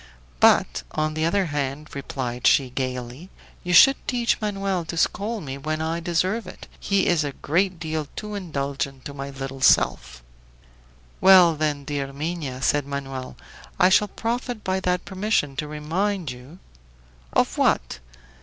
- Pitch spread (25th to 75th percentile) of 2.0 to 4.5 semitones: No, wide, 5.4 semitones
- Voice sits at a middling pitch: Yes, medium, 155 Hz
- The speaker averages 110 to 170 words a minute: Yes, average, 155 wpm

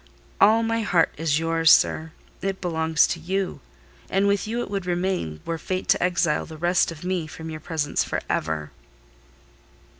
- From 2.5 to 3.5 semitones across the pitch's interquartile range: Yes, average, 3.0 semitones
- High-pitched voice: No, medium, 170 Hz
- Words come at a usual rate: Yes, average, 175 wpm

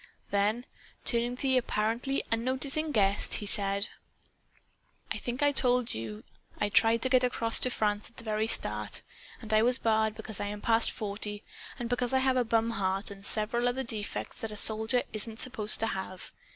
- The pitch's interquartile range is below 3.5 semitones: Yes, average, 2.9 semitones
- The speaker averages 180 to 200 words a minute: Yes, average, 190 wpm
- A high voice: Yes, high, 225 Hz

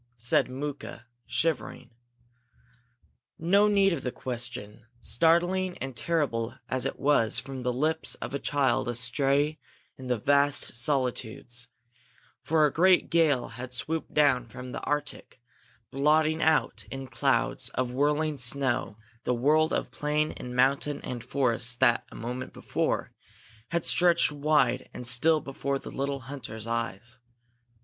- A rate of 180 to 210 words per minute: No, average, 140 wpm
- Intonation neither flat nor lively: Yes, average, 3.7 semitones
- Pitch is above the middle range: No, low, 135 Hz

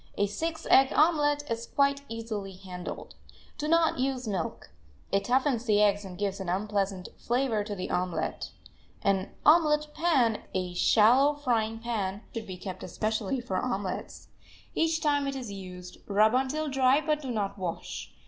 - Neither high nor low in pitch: No, high, 225 Hz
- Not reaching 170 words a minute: Yes, average, 160 wpm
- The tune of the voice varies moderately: No, wide, 5.9 semitones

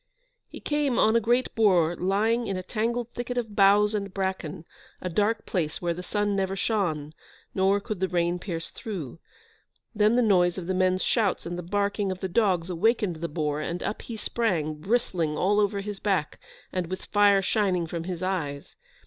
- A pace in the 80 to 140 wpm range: No, average, 190 wpm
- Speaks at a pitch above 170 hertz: Yes, high, 190 Hz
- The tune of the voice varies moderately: Yes, average, 3.3 semitones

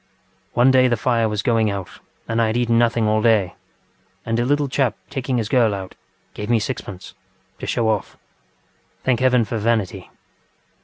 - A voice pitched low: Yes, low, 115 Hz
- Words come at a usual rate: Yes, average, 170 wpm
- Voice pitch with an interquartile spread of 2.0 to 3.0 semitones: Yes, narrow, 2.4 semitones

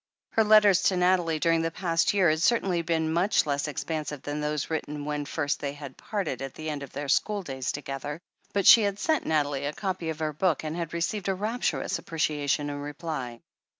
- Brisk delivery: Yes, fast, 210 wpm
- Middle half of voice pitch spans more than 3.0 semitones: Yes, average, 4.0 semitones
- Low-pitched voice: No, medium, 160 Hz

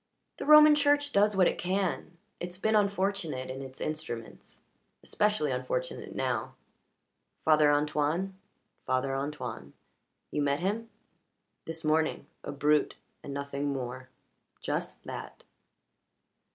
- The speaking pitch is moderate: Yes, medium, 150 Hz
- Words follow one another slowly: Yes, slow, 115 wpm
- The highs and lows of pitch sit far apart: Yes, wide, 6.2 semitones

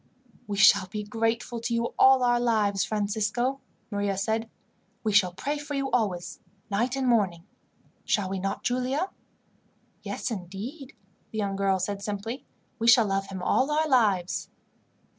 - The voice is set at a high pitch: Yes, high, 220 Hz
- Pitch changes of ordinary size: Yes, average, 3.9 semitones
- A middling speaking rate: Yes, average, 155 wpm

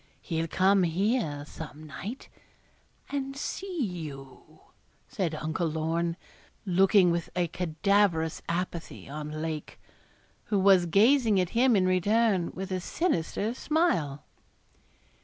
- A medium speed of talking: No, slow, 115 wpm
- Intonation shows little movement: No, average, 4.4 semitones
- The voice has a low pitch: No, medium, 180 Hz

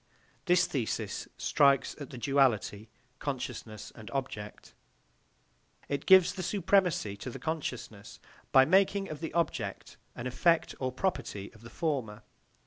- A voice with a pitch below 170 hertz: Yes, low, 135 Hz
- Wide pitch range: Yes, wide, 6.5 semitones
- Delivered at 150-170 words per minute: No, slow, 135 wpm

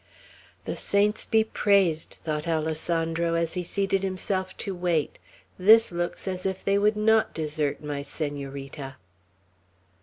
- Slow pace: Yes, slow, 130 wpm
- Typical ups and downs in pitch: Yes, average, 4.2 semitones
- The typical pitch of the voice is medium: Yes, medium, 175 Hz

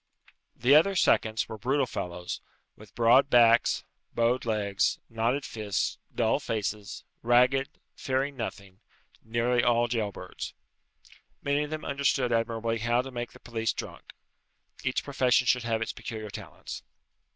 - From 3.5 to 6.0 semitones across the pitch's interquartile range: No, average, 2.7 semitones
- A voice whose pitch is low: Yes, low, 120 Hz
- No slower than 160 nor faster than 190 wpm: No, average, 140 wpm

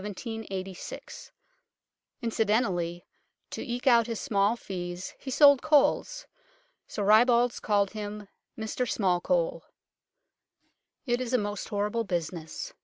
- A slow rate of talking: Yes, slow, 110 wpm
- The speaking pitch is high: Yes, high, 220 Hz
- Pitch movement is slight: No, average, 3.9 semitones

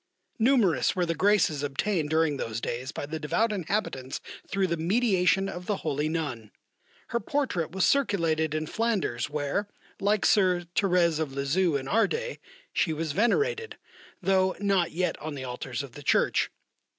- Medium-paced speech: Yes, average, 160 wpm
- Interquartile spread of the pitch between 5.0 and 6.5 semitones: Yes, wide, 5.5 semitones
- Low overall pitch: No, medium, 170 Hz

